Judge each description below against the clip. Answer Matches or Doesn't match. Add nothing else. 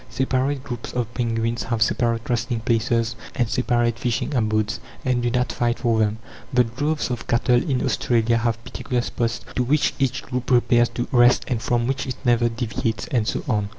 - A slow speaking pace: Doesn't match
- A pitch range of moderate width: Doesn't match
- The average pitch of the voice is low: Matches